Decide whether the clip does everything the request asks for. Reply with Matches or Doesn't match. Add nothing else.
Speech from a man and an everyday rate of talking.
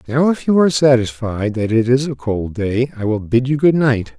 Doesn't match